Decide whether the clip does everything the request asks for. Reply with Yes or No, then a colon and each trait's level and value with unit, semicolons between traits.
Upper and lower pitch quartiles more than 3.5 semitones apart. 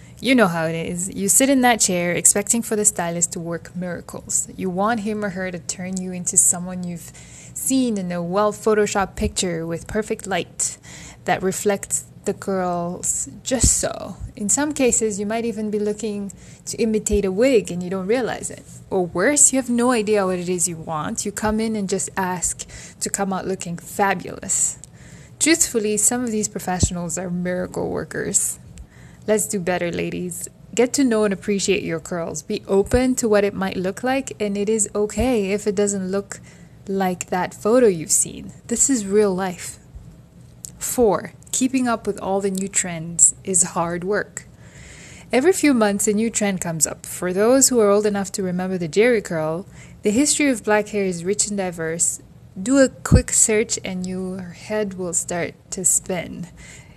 No: average, 3.2 semitones